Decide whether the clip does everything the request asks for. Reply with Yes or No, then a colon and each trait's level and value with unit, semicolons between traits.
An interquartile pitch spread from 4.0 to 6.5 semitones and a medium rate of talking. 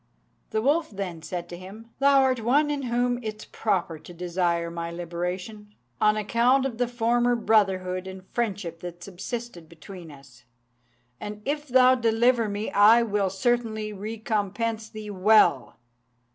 Yes: average, 4.5 semitones; average, 150 wpm